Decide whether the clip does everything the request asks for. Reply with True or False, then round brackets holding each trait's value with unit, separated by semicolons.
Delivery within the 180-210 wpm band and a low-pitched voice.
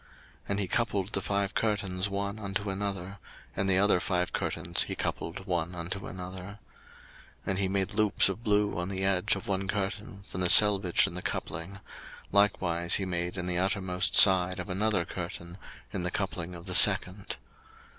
True (185 wpm; 95 Hz)